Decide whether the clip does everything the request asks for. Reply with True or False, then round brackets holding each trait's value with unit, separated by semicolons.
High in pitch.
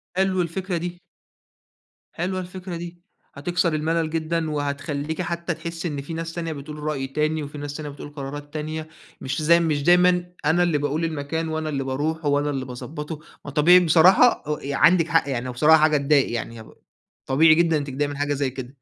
False (155 Hz)